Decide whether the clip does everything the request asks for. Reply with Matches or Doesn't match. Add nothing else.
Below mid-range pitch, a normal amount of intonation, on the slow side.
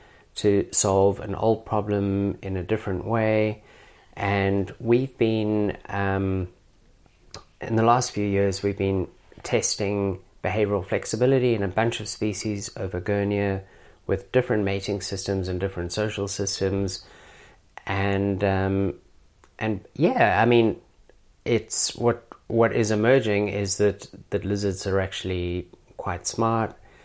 Doesn't match